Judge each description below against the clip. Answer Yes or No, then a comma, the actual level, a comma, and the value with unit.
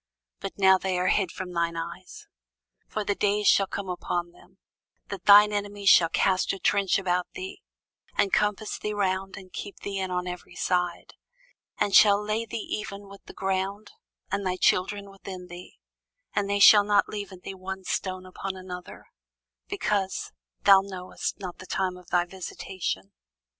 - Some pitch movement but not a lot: No, narrow, 1.9 semitones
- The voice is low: No, high, 190 Hz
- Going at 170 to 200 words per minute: Yes, average, 175 wpm